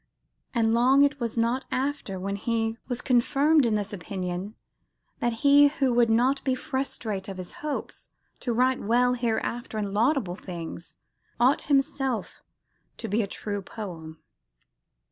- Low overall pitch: No, high, 235 Hz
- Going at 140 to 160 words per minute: Yes, average, 145 wpm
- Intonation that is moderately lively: Yes, average, 4.4 semitones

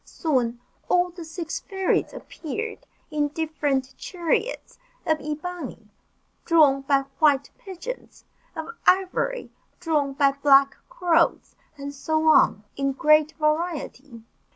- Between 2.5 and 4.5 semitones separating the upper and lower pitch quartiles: Yes, average, 4.0 semitones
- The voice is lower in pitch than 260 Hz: No, very high, 310 Hz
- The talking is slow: Yes, slow, 110 wpm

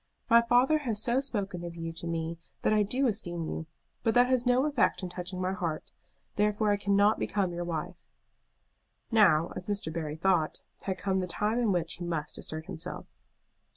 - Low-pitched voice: No, high, 190 Hz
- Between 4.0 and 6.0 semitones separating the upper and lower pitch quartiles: Yes, average, 4.7 semitones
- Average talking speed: Yes, average, 190 wpm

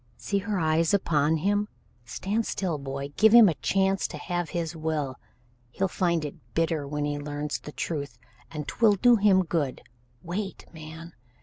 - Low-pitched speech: No, medium, 165 Hz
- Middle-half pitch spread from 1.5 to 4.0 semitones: No, average, 4.5 semitones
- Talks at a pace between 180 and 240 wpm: No, average, 170 wpm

